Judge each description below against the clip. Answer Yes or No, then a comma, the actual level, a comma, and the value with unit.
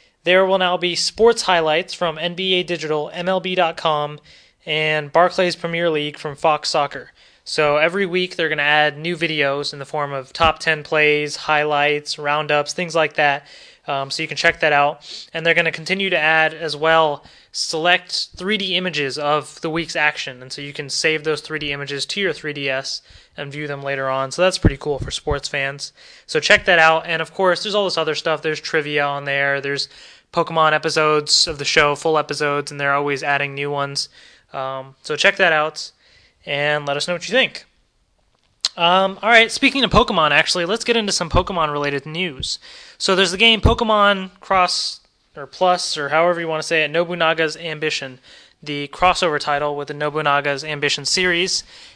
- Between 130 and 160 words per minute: No, average, 190 wpm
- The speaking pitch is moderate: Yes, medium, 155 Hz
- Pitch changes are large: No, average, 3.4 semitones